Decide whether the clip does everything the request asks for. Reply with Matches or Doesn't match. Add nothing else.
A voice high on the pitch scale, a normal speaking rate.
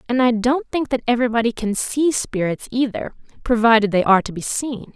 Matches